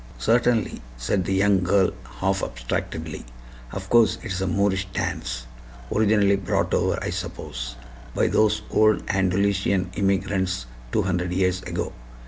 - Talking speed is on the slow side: Yes, slow, 130 wpm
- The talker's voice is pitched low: Yes, very low, 95 Hz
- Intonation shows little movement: Yes, narrow, 2.0 semitones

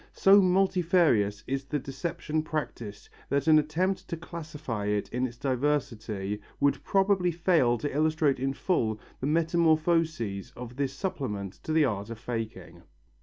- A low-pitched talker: No, medium, 145 Hz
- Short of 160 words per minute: Yes, average, 145 wpm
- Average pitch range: No, wide, 5.8 semitones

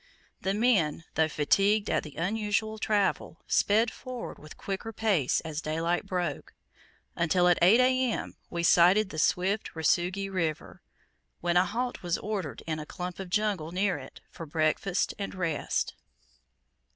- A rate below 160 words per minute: Yes, average, 150 wpm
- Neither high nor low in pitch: Yes, medium, 180 Hz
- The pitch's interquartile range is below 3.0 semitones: No, average, 4.2 semitones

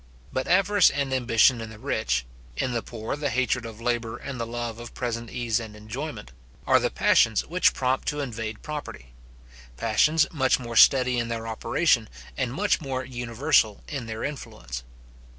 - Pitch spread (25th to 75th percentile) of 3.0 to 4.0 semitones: Yes, average, 3.3 semitones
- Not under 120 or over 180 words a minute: Yes, average, 170 wpm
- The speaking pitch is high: No, low, 120 Hz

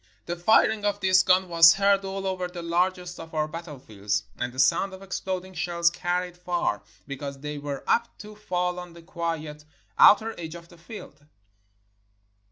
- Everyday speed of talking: Yes, average, 175 wpm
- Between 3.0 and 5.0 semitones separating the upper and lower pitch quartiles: No, narrow, 2.5 semitones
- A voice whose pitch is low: No, medium, 175 Hz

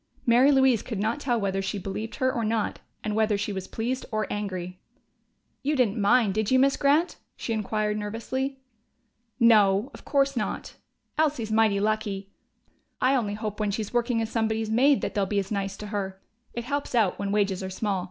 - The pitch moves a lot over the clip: No, average, 3.4 semitones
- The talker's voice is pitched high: Yes, high, 220 Hz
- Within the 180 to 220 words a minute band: Yes, average, 190 wpm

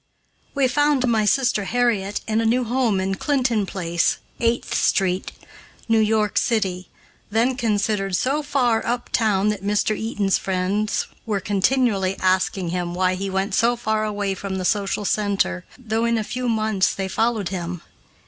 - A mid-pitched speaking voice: No, high, 210 Hz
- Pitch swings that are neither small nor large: Yes, average, 3.4 semitones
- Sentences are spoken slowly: No, average, 160 wpm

